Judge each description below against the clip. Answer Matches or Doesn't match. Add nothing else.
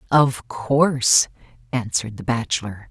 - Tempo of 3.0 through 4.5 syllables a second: Matches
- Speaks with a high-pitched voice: Doesn't match